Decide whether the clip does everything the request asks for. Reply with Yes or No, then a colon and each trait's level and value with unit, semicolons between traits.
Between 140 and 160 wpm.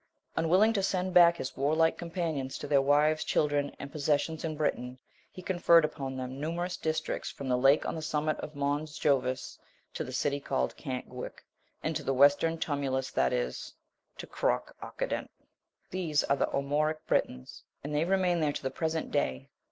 No: average, 180 wpm